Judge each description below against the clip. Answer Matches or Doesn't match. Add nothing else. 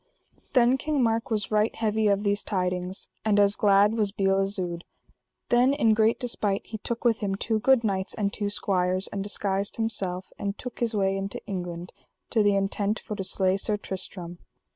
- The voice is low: Doesn't match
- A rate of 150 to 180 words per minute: Doesn't match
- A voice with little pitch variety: Matches